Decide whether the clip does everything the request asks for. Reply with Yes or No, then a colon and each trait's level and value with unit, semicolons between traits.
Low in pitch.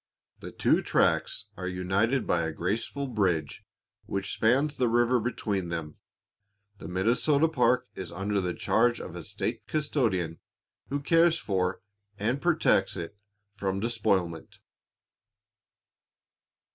Yes: low, 105 Hz